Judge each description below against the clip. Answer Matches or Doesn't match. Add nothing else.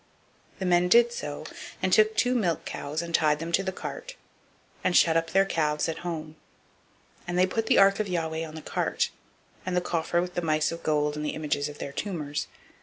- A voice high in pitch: Doesn't match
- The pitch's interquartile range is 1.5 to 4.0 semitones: Matches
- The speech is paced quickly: Matches